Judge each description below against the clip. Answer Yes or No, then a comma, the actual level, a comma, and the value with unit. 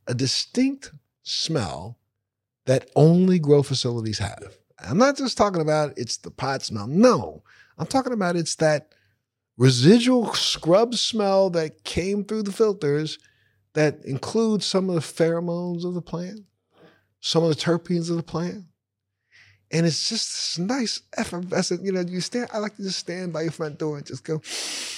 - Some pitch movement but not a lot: No, wide, 6.5 semitones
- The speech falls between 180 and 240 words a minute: No, average, 170 wpm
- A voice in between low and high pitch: Yes, medium, 165 Hz